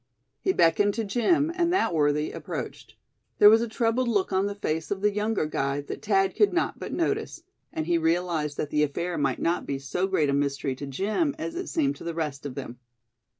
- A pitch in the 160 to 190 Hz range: Yes, medium, 185 Hz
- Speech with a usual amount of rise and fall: No, wide, 7.1 semitones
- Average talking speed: No, fast, 220 wpm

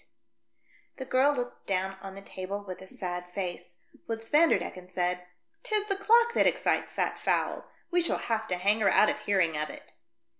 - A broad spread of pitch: Yes, wide, 6.3 semitones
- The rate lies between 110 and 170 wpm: No, average, 195 wpm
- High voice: Yes, high, 200 Hz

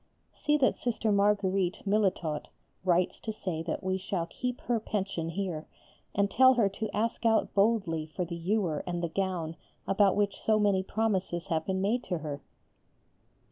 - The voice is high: Yes, high, 195 Hz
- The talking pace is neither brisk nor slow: Yes, average, 170 wpm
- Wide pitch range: No, average, 3.7 semitones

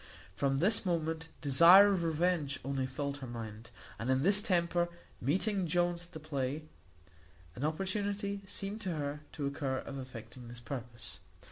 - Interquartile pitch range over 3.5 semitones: Yes, average, 5.2 semitones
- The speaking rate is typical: Yes, average, 155 wpm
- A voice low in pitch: No, medium, 155 Hz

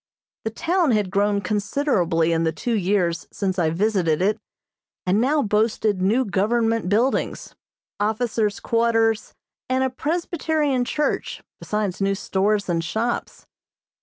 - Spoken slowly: Yes, slow, 130 wpm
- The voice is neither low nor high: No, high, 210 Hz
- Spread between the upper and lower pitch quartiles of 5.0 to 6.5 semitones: No, average, 4.0 semitones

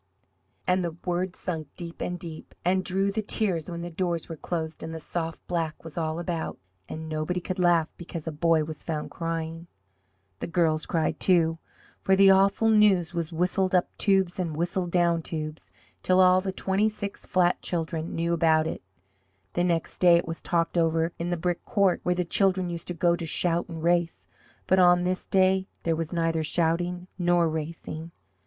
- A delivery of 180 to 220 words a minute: Yes, average, 190 wpm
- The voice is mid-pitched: Yes, medium, 170 Hz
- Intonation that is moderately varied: No, narrow, 1.9 semitones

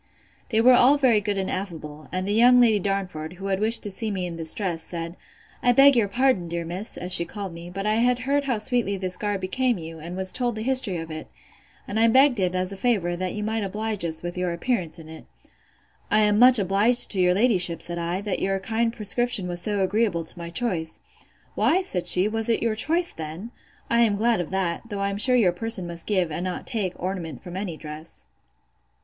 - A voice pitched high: Yes, high, 195 Hz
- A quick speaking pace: Yes, fast, 230 wpm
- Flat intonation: No, average, 4.5 semitones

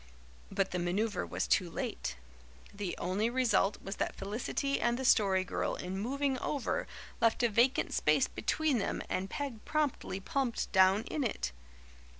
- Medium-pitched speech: No, high, 220 Hz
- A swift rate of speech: No, average, 155 wpm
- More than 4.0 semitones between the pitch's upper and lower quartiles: Yes, average, 5.2 semitones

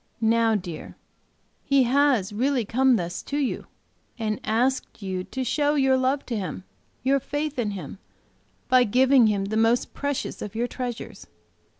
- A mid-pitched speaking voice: No, high, 245 Hz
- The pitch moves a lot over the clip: No, average, 4.1 semitones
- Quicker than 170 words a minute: No, average, 160 wpm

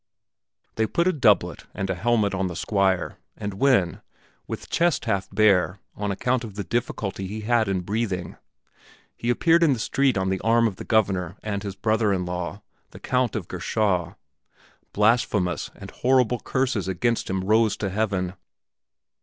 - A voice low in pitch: Yes, low, 105 Hz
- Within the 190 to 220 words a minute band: No, average, 170 wpm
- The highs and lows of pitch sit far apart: No, average, 3.6 semitones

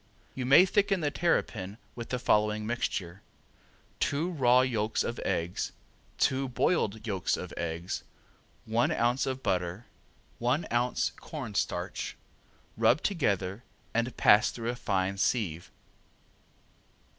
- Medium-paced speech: No, slow, 120 wpm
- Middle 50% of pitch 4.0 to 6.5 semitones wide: Yes, average, 4.9 semitones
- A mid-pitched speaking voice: No, low, 120 Hz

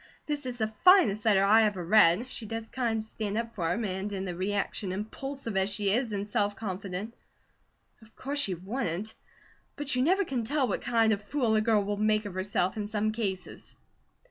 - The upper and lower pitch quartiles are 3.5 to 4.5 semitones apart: No, average, 2.8 semitones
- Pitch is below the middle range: No, high, 215 Hz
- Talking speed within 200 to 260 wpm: Yes, fast, 205 wpm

